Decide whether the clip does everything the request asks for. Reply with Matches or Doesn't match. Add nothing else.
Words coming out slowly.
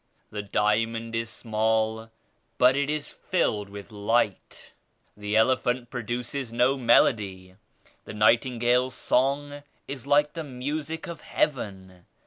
Matches